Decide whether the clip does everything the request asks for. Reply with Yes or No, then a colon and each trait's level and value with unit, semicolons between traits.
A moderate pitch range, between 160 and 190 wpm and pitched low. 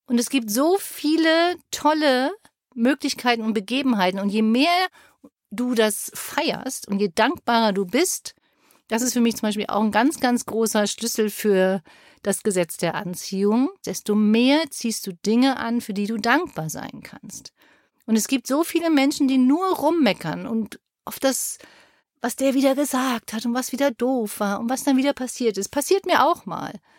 No: average, 4.7 semitones; average, 180 wpm; high, 245 Hz